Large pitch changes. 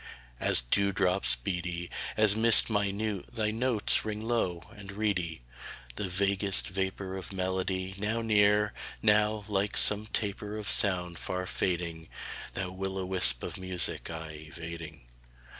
No: average, 3.0 semitones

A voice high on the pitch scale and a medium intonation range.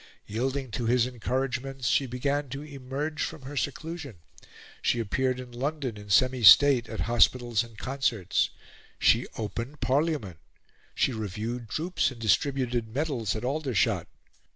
No: low, 125 Hz; average, 3.1 semitones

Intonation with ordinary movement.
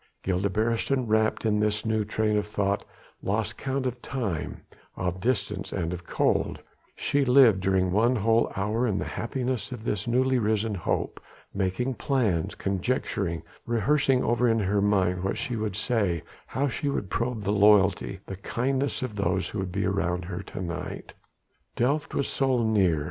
Yes: average, 4.2 semitones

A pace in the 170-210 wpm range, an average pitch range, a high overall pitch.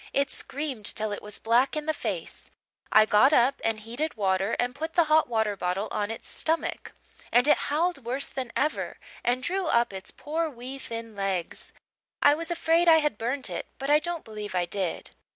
No: average, 200 wpm; wide, 6.0 semitones; very high, 250 Hz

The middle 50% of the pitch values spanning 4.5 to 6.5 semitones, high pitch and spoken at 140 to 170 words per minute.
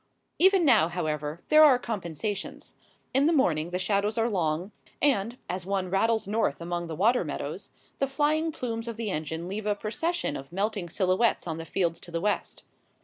No: average, 5.3 semitones; high, 200 Hz; average, 185 wpm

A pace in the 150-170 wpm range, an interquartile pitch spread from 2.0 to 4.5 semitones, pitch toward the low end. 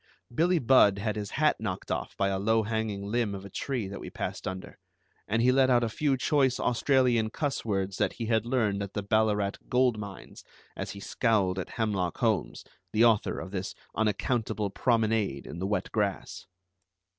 No: average, 190 wpm; average, 3.3 semitones; low, 110 Hz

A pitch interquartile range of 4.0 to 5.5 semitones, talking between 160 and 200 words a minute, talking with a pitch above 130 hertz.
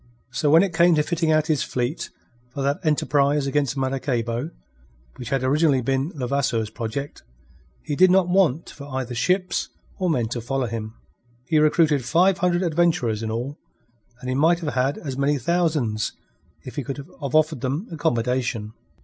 Yes: average, 4.3 semitones; average, 170 wpm; medium, 140 Hz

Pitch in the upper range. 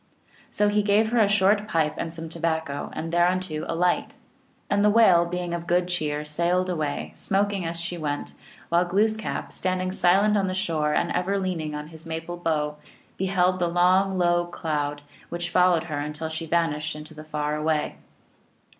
No: medium, 175 Hz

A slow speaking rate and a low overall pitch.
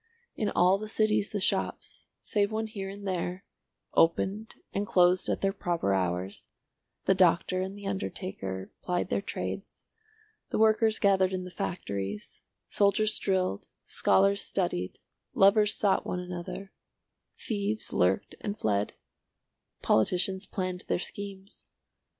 No: slow, 130 wpm; high, 190 Hz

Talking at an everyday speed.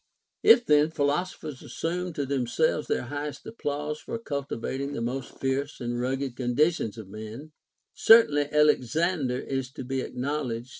Yes: average, 165 wpm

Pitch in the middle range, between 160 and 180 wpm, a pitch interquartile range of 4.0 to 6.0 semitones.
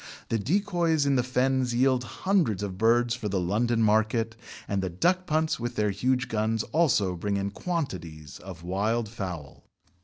No: low, 115 Hz; average, 165 wpm; average, 4.9 semitones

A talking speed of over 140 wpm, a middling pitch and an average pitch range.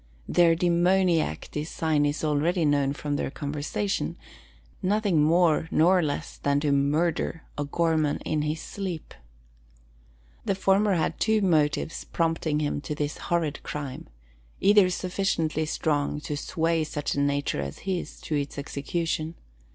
No: slow, 135 wpm; medium, 155 Hz; average, 3.0 semitones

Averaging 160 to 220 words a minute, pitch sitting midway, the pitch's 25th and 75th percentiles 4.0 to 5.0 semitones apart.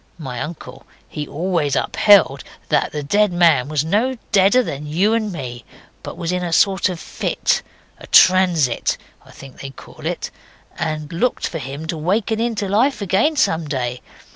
No: average, 170 wpm; medium, 170 Hz; wide, 5.4 semitones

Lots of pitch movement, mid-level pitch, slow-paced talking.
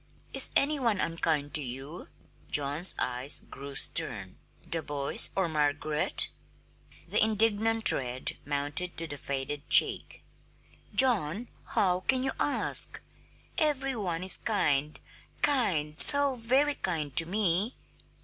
Yes: wide, 7.7 semitones; medium, 165 Hz; slow, 120 wpm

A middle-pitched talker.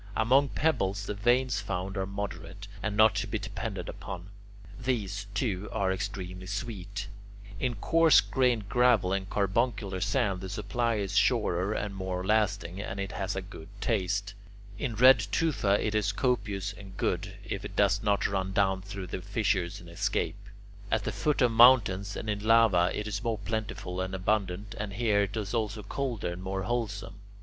No: low, 100 Hz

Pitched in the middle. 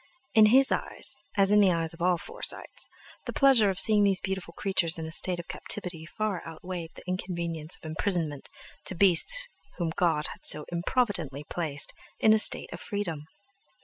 Yes: medium, 180 Hz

